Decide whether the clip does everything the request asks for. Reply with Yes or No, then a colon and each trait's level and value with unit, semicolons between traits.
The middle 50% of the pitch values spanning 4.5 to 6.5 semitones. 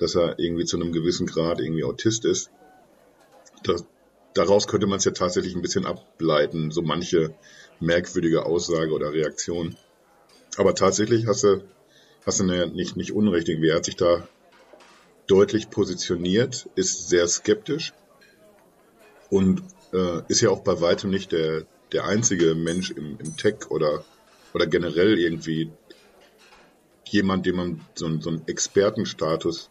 No: average, 3.4 semitones